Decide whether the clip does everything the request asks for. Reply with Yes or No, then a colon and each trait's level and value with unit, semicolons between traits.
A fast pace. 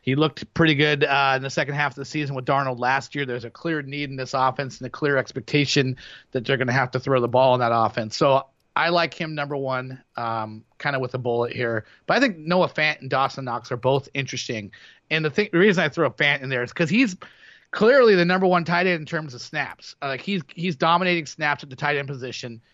Yes: fast, 260 wpm